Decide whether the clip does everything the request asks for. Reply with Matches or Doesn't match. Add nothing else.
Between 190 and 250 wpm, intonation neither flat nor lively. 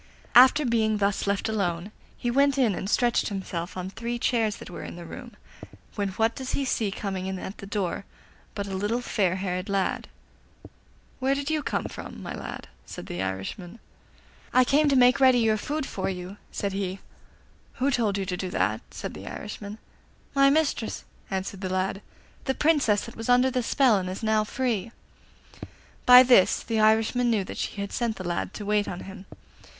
Matches